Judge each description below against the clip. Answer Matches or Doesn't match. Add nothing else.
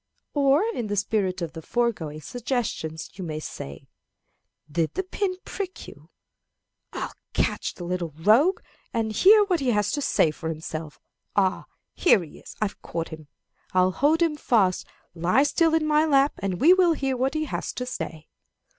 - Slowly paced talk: Doesn't match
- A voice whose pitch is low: Doesn't match